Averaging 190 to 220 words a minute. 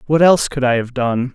No: fast, 270 wpm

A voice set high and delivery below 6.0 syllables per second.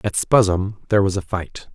No: very low, 95 Hz; 5.2 syllables/s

